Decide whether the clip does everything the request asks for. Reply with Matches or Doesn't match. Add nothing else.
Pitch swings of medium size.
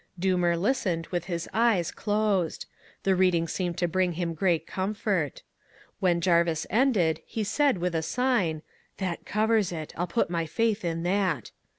Matches